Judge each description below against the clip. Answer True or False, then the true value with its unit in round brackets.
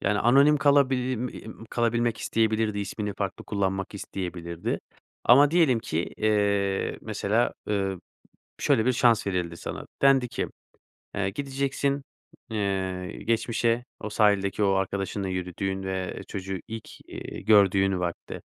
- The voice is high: False (105 Hz)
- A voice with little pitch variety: False (3.5 semitones)